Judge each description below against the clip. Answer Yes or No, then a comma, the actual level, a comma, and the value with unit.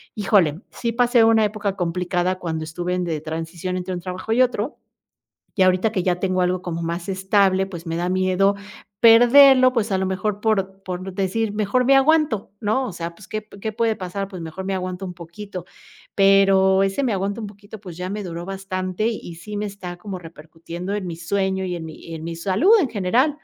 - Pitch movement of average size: Yes, average, 3.0 semitones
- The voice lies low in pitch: No, high, 190 Hz